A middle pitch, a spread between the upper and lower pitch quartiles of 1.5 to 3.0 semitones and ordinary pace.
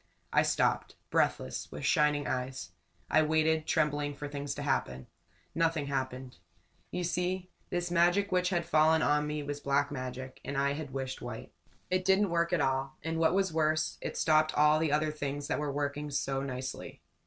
Yes: medium, 150 Hz; average, 2.7 semitones; average, 180 wpm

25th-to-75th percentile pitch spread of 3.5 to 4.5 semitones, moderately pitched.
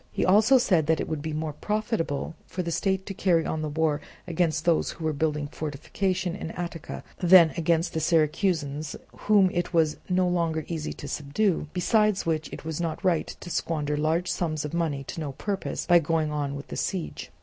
No: average, 2.8 semitones; medium, 165 Hz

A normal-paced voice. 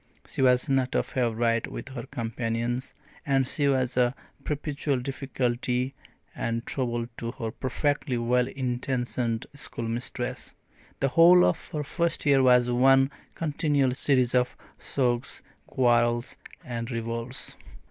No: slow, 125 wpm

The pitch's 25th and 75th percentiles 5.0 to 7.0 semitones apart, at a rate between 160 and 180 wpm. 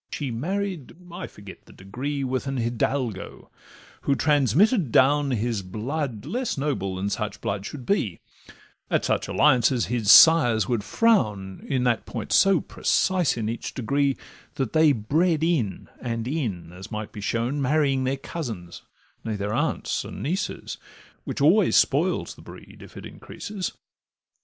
No: wide, 5.6 semitones; average, 150 wpm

